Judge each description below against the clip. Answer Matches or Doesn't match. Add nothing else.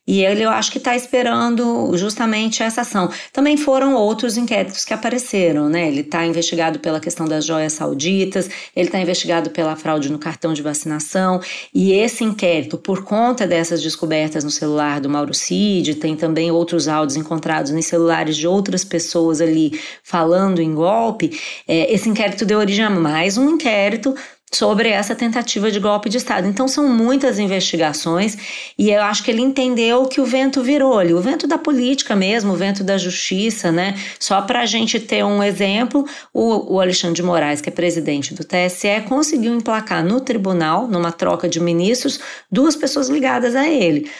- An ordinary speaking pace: Matches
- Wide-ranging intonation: Matches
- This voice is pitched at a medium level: Doesn't match